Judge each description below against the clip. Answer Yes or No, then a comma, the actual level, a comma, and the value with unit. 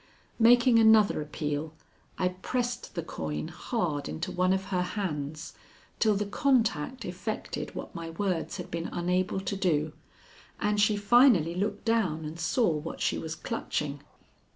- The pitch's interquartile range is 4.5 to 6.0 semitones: Yes, average, 5.0 semitones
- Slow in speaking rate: No, average, 150 wpm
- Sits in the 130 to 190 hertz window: Yes, medium, 185 Hz